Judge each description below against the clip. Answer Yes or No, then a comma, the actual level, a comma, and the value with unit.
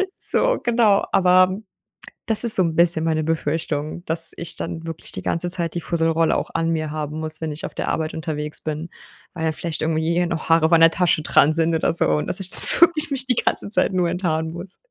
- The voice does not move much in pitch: Yes, narrow, 2.1 semitones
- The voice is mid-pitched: Yes, medium, 165 Hz